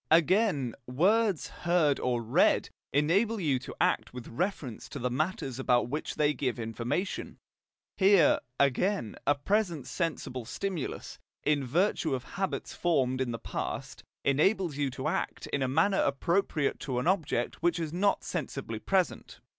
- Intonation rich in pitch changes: Yes, wide, 6.2 semitones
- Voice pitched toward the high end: No, medium, 150 Hz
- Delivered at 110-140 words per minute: No, average, 150 wpm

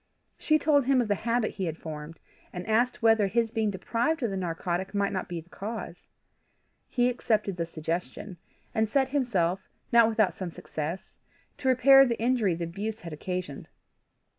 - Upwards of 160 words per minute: Yes, average, 175 wpm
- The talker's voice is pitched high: Yes, high, 205 Hz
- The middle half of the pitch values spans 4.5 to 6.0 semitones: Yes, average, 5.1 semitones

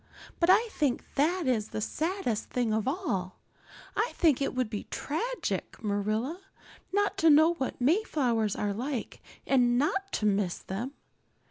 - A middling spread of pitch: No, wide, 7.7 semitones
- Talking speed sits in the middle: Yes, average, 150 wpm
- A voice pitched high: Yes, very high, 265 Hz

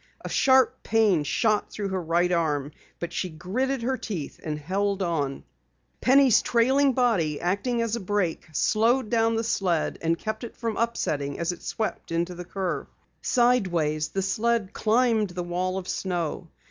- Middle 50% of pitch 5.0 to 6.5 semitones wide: Yes, average, 5.3 semitones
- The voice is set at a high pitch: Yes, high, 195 Hz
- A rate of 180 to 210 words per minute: No, average, 160 wpm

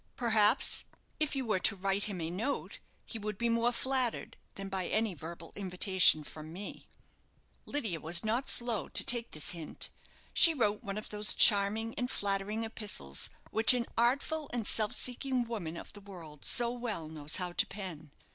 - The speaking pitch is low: No, high, 210 Hz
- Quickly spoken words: No, average, 175 wpm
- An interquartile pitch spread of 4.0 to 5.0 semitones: Yes, average, 4.5 semitones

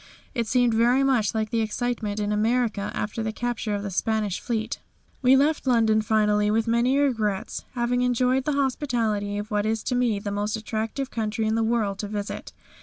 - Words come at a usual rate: Yes, average, 190 wpm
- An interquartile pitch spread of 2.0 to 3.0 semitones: Yes, average, 2.7 semitones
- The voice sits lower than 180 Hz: No, high, 225 Hz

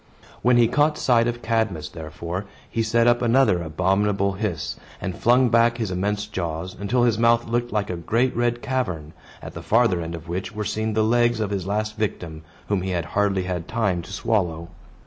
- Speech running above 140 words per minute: Yes, average, 200 wpm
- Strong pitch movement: No, average, 4.4 semitones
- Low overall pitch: Yes, low, 105 Hz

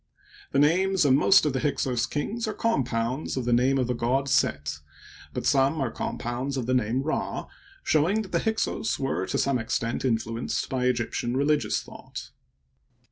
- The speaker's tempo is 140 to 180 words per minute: Yes, average, 175 wpm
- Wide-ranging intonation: No, average, 3.7 semitones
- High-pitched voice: No, low, 130 Hz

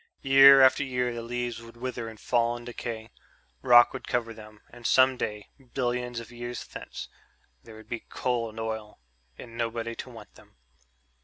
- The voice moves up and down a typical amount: No, narrow, 1.3 semitones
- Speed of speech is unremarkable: Yes, average, 175 wpm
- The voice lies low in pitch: Yes, low, 120 Hz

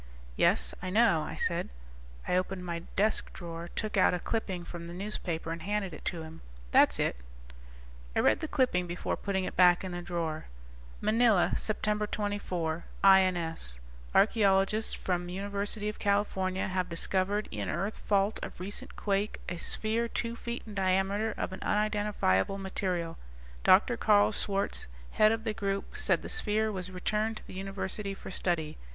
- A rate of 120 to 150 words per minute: No, average, 165 wpm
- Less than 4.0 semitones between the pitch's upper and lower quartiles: Yes, average, 3.1 semitones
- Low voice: No, high, 195 Hz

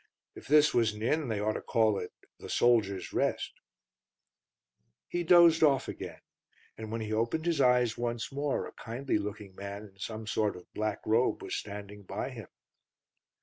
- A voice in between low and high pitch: No, low, 110 Hz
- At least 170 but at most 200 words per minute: Yes, average, 175 wpm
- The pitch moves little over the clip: No, average, 4.2 semitones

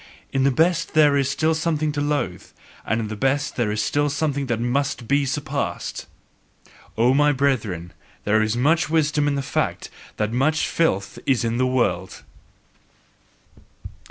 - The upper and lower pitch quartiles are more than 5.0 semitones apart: No, average, 4.3 semitones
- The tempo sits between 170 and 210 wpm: No, average, 155 wpm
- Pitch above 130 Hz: Yes, medium, 140 Hz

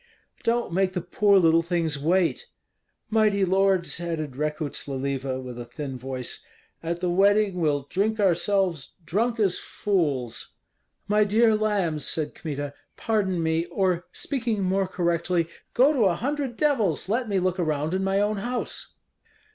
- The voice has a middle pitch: Yes, medium, 180 Hz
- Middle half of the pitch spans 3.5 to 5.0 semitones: Yes, average, 4.7 semitones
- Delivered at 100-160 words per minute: Yes, average, 150 wpm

